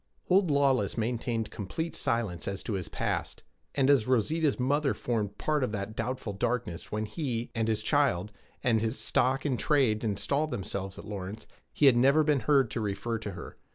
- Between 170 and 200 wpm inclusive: Yes, average, 185 wpm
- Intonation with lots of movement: No, average, 4.8 semitones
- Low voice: Yes, low, 115 Hz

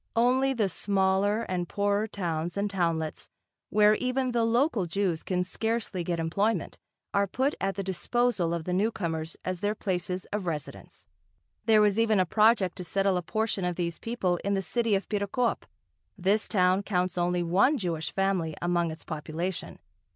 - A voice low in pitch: No, high, 195 Hz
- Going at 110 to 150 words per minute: No, average, 170 wpm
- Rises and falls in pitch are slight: No, average, 3.5 semitones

